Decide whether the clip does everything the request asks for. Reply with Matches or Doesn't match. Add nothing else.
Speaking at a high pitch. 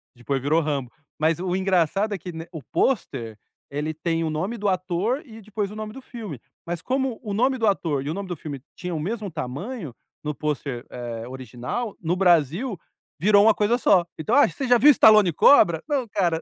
Doesn't match